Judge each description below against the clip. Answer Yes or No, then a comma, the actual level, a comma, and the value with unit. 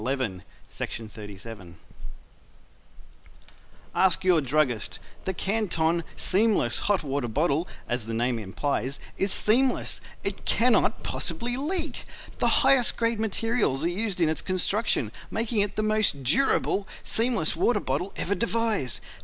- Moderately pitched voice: Yes, medium, 180 Hz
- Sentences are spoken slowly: Yes, slow, 125 wpm